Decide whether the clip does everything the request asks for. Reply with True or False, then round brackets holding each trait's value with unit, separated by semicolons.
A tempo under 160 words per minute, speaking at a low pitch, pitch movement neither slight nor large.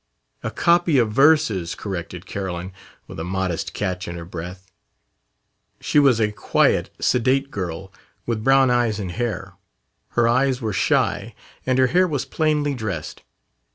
False (150 wpm; 110 Hz; 6.4 semitones)